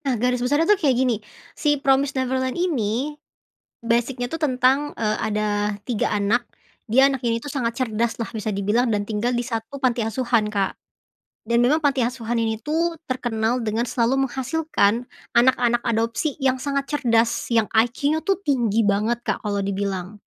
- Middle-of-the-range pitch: No, high, 240 Hz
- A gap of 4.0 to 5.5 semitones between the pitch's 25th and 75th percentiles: No, average, 3.3 semitones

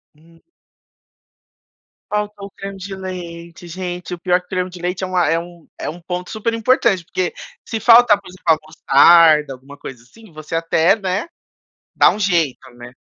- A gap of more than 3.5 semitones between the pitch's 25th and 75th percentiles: No, average, 2.8 semitones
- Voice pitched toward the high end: No, medium, 180 Hz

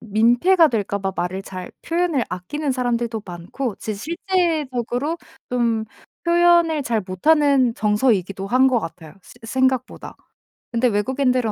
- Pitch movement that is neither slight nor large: No, wide, 5.7 semitones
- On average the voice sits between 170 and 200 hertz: No, high, 245 Hz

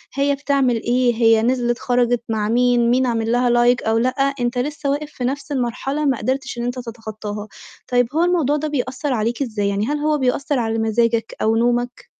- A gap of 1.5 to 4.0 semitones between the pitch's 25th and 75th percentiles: Yes, average, 3.0 semitones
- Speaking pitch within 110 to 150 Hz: No, high, 245 Hz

